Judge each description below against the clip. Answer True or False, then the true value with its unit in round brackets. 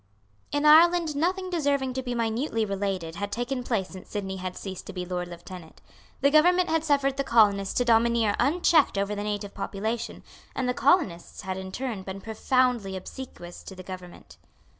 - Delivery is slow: False (180 wpm)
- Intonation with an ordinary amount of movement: False (6.4 semitones)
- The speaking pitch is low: False (225 Hz)